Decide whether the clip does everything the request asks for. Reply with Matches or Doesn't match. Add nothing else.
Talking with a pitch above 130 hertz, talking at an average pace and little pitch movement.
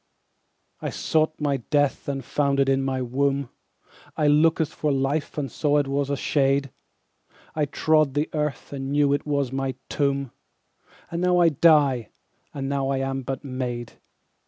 Matches